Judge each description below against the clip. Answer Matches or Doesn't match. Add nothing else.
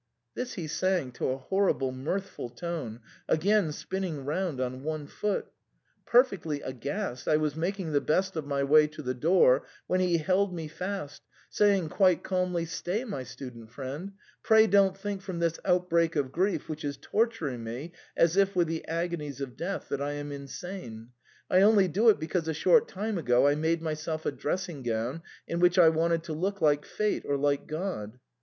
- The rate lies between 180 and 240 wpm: Matches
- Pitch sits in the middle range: Matches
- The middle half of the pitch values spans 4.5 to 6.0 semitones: Matches